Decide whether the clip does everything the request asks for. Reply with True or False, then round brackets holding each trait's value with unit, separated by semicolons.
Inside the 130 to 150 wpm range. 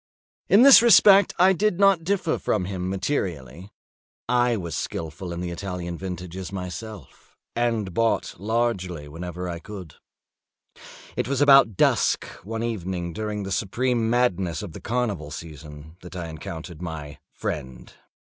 True (140 wpm)